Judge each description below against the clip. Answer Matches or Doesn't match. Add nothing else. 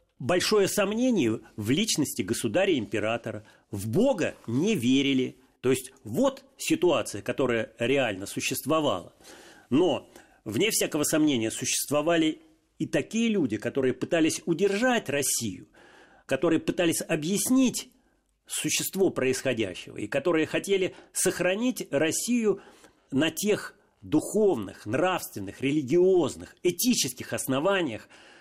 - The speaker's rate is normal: Doesn't match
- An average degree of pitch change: Doesn't match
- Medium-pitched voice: Matches